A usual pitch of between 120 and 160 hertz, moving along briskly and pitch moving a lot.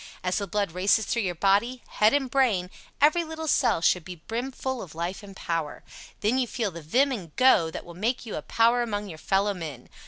No: high, 205 Hz; fast, 225 wpm; wide, 5.7 semitones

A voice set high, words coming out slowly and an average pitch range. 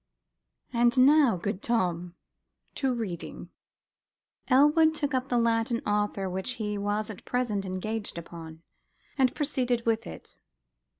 Yes: high, 225 Hz; slow, 125 wpm; average, 4.4 semitones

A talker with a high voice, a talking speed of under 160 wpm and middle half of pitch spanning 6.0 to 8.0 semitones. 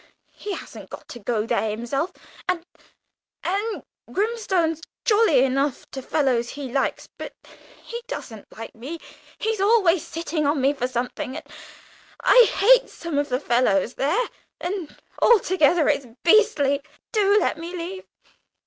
Yes: very high, 320 Hz; average, 140 wpm; wide, 7.1 semitones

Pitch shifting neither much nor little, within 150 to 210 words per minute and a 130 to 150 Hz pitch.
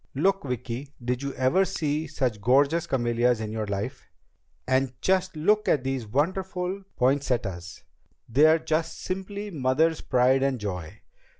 No: average, 4.9 semitones; slow, 135 wpm; low, 135 Hz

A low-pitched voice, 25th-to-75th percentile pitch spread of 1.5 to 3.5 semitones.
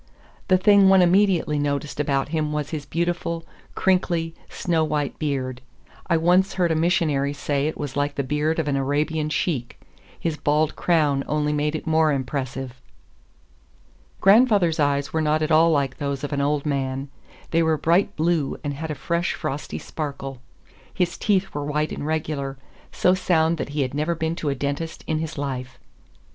No: medium, 150 Hz; average, 2.7 semitones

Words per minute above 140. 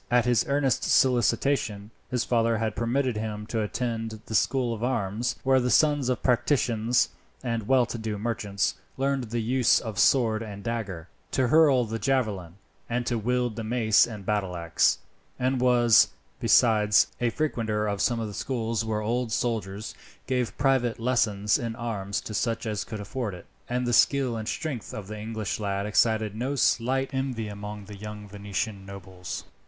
Yes: average, 170 wpm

